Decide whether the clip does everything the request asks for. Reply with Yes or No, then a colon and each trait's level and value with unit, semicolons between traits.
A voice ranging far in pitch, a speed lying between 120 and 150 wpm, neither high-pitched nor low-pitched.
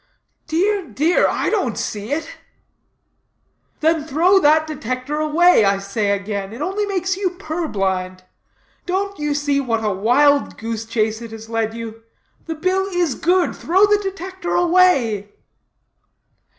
No: wide, 8.2 semitones; average, 140 wpm; very high, 295 Hz